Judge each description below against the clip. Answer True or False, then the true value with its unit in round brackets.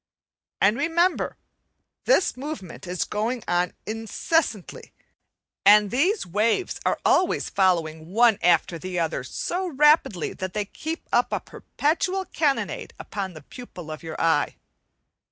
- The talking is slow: True (130 wpm)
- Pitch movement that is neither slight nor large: False (9.0 semitones)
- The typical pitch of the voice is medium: False (210 Hz)